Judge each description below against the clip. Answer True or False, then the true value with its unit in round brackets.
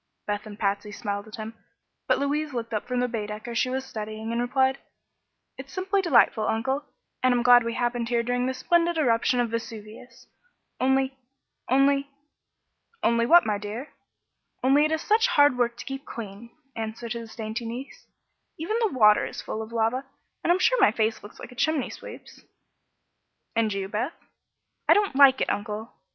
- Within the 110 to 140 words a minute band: False (180 wpm)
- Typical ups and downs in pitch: True (3.7 semitones)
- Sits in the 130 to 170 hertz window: False (240 Hz)